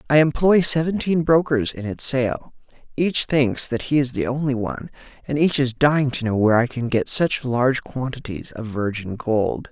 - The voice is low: Yes, low, 130 Hz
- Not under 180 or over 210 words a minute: Yes, average, 190 wpm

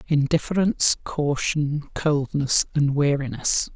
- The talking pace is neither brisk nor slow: No, slow, 80 wpm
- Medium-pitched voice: Yes, medium, 145 Hz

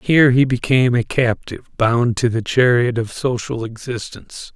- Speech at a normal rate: Yes, average, 160 wpm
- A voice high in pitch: No, low, 120 Hz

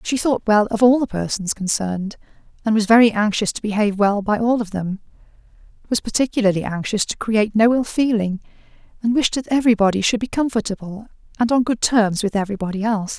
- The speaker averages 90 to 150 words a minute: No, average, 180 wpm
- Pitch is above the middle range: Yes, high, 215 Hz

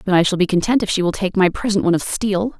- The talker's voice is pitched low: No, high, 195 Hz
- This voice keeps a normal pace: No, fast, 325 wpm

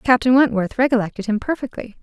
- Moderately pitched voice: No, high, 235 Hz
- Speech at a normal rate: Yes, average, 150 wpm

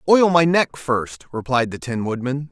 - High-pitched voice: No, low, 135 Hz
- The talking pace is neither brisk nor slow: Yes, average, 190 wpm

